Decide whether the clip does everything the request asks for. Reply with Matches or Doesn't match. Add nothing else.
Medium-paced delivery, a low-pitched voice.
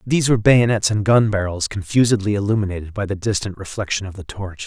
Matches